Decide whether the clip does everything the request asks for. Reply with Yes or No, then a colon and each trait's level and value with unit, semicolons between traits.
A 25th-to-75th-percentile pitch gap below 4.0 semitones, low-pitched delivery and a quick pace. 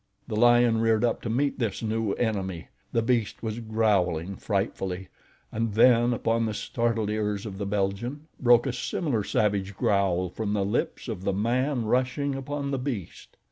No: average, 3.2 semitones; low, 110 Hz; average, 170 wpm